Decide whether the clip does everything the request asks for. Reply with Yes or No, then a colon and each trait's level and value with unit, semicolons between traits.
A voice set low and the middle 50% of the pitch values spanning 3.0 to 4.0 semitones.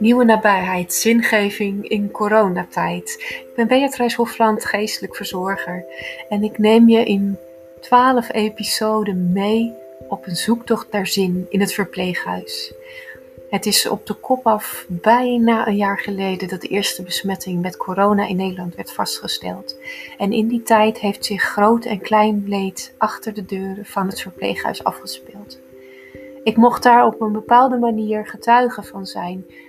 No: high, 210 Hz; average, 3.5 semitones